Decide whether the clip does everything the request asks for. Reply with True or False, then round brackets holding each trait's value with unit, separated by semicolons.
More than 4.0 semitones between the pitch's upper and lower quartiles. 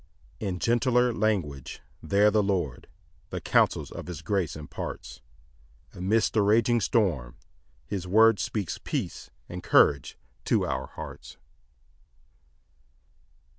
True (4.6 semitones)